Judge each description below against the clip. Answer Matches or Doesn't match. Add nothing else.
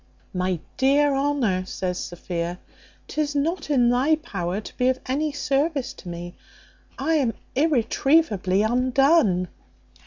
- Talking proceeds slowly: Matches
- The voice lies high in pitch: Matches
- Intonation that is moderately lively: Doesn't match